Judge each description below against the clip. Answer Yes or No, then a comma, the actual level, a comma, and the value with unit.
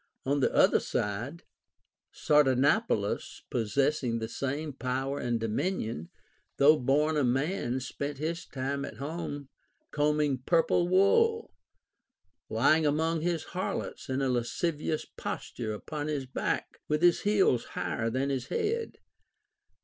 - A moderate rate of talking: No, slow, 125 wpm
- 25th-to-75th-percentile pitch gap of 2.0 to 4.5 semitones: Yes, average, 4.0 semitones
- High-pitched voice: No, medium, 140 Hz